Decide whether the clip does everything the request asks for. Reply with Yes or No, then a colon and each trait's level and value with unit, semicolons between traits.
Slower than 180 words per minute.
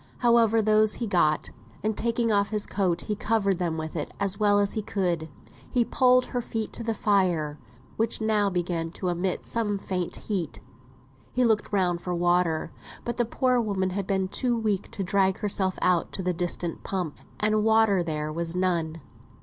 No: average, 185 wpm